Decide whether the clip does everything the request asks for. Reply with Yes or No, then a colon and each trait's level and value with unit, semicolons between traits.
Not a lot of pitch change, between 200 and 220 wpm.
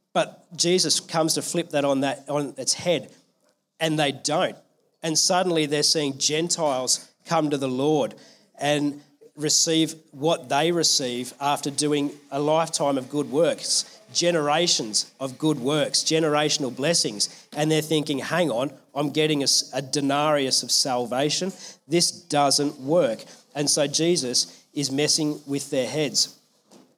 No: narrow, 2.2 semitones; average, 140 wpm